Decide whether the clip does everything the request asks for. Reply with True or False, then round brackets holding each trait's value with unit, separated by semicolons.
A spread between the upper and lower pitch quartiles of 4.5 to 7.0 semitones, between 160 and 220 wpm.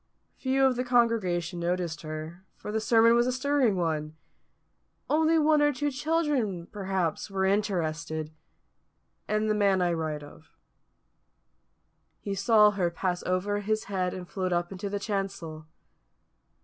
False (4.9 semitones; 145 wpm)